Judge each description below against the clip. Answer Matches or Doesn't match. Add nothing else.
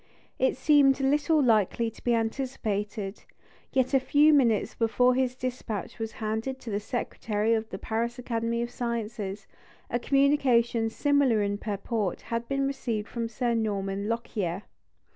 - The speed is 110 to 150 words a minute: Matches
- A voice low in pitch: Doesn't match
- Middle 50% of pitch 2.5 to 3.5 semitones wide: Matches